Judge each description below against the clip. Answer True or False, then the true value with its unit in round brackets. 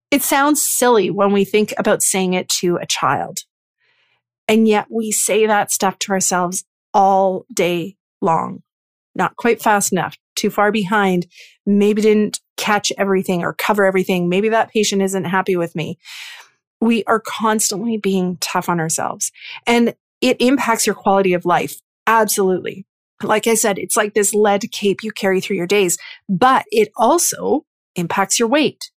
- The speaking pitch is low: False (205 Hz)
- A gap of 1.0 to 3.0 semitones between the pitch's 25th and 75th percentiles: True (2.7 semitones)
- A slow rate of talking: False (160 wpm)